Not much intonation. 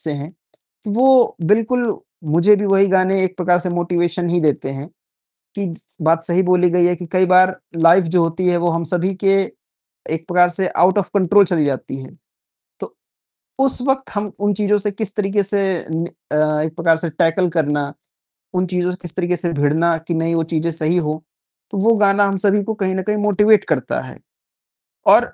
No: average, 3.2 semitones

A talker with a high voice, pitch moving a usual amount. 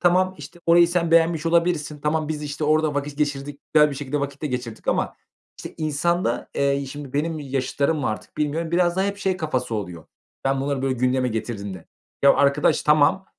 No: medium, 145 Hz; average, 3.2 semitones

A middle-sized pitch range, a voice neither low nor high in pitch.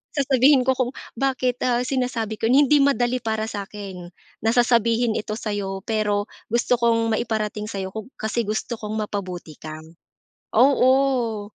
No: average, 3.1 semitones; high, 225 Hz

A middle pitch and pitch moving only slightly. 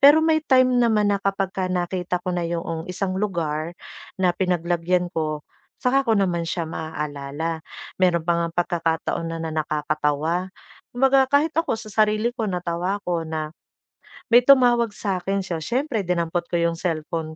No: medium, 180 Hz; average, 4.3 semitones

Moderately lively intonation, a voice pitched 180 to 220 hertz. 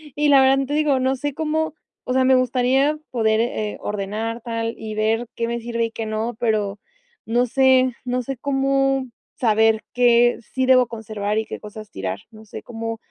No: average, 3.0 semitones; high, 235 Hz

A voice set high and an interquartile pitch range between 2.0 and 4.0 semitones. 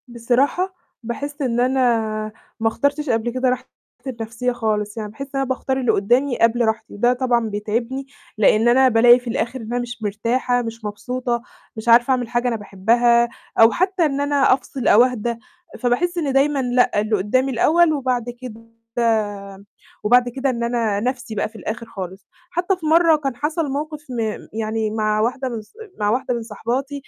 Yes: high, 240 Hz; average, 2.9 semitones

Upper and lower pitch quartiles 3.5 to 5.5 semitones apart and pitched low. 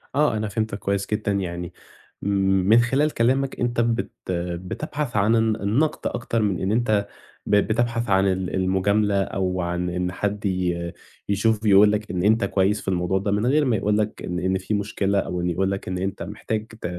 No: average, 2.8 semitones; low, 100 Hz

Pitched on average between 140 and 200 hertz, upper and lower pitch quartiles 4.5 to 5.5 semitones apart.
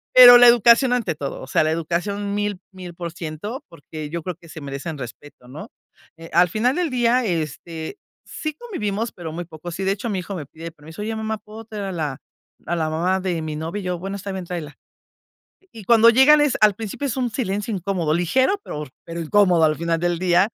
Yes: medium, 185 Hz; average, 5.1 semitones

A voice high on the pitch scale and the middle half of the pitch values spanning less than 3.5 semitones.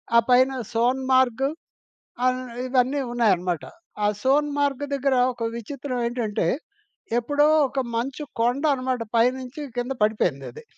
Yes: very high, 255 Hz; narrow, 2.5 semitones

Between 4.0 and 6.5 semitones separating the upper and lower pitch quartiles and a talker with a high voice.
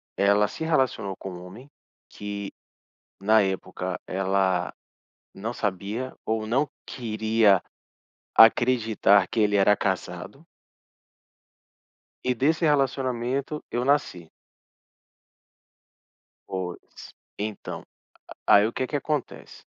No: average, 4.7 semitones; low, 110 Hz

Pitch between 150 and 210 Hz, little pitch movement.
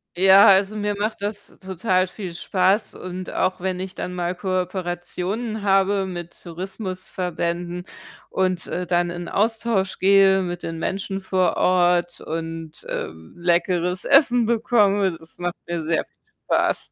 Yes: medium, 185 Hz; narrow, 2.0 semitones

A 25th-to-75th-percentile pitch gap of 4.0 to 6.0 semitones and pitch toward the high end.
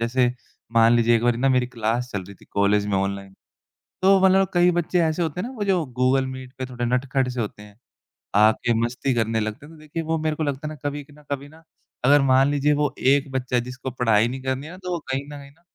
No: average, 4.3 semitones; low, 130 Hz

